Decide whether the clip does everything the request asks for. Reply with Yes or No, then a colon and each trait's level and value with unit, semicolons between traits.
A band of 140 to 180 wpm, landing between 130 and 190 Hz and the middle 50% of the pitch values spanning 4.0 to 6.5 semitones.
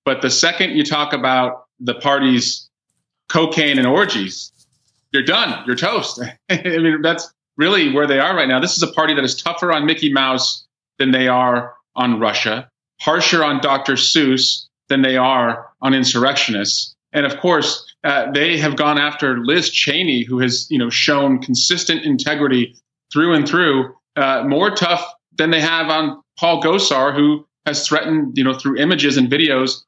No: average, 175 wpm; low, 135 Hz; average, 3.5 semitones